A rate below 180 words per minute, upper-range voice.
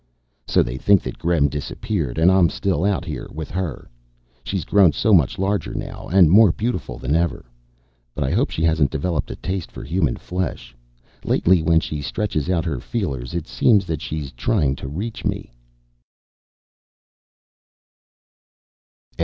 No: average, 155 wpm; very low, 80 Hz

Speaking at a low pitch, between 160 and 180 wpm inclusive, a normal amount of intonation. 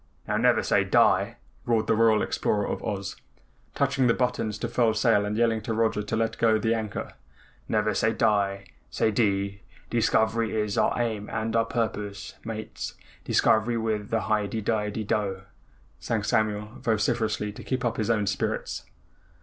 No: low, 110 Hz; average, 175 wpm; narrow, 1.5 semitones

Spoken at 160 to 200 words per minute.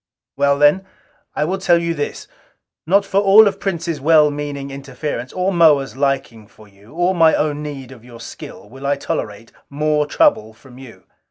Yes: average, 180 wpm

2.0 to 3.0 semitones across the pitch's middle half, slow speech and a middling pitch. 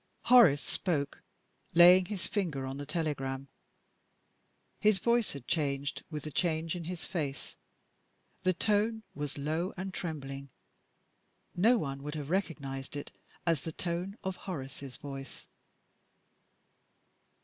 No: average, 4.8 semitones; slow, 125 wpm; medium, 160 Hz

